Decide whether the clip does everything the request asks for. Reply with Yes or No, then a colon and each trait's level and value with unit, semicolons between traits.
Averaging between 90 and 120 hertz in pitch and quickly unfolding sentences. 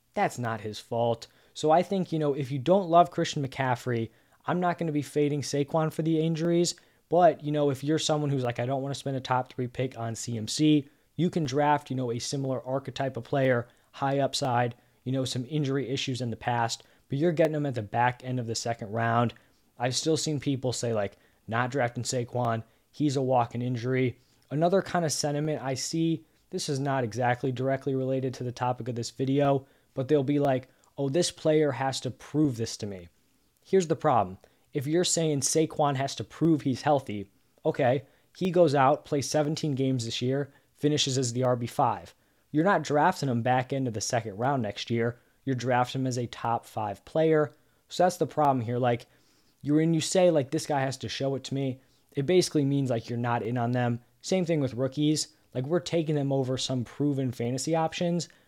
No: low, 135 Hz; fast, 210 wpm